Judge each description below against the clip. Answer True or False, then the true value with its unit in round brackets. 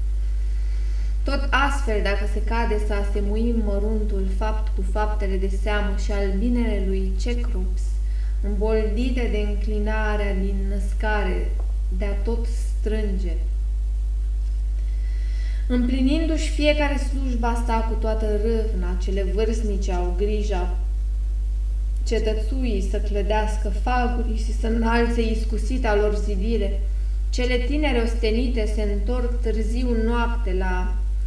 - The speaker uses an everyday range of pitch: True (3.9 semitones)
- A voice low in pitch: False (210 Hz)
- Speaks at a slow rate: True (105 wpm)